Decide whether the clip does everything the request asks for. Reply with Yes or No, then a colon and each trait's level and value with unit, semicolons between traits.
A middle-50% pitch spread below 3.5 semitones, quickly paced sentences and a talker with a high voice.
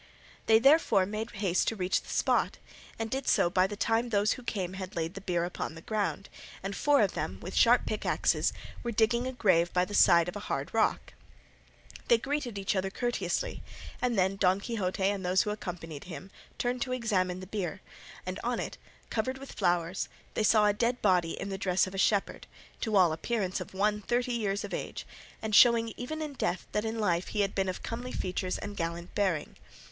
No: average, 3.9 semitones; fast, 210 wpm; high, 200 Hz